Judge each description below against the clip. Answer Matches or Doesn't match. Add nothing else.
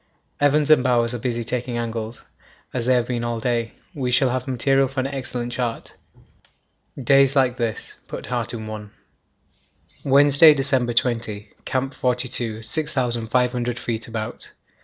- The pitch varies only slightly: Matches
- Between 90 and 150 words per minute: Matches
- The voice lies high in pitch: Doesn't match